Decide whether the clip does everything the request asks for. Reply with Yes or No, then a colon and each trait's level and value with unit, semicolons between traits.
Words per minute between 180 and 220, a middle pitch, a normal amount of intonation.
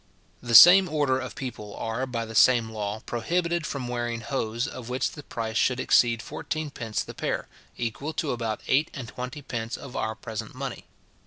No: average, 185 wpm; low, 120 Hz; average, 3.4 semitones